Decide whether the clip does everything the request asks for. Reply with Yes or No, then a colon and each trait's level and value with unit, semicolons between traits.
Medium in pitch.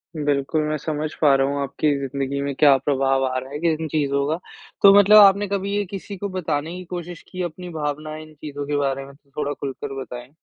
Yes: medium, 150 Hz